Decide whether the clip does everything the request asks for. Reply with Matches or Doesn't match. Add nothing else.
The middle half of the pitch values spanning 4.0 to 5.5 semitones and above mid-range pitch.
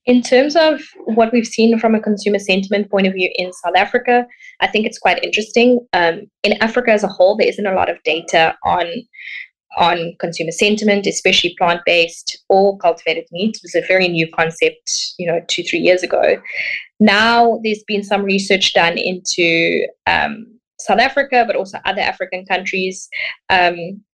Matches